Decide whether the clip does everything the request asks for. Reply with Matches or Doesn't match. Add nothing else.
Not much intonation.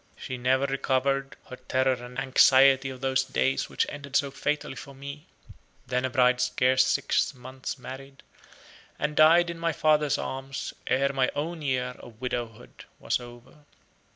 Matches